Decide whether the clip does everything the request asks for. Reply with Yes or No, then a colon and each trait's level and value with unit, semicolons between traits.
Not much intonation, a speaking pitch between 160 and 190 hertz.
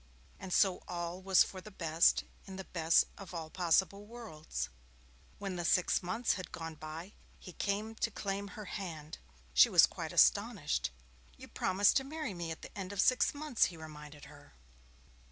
No: average, 3.7 semitones; medium, 185 Hz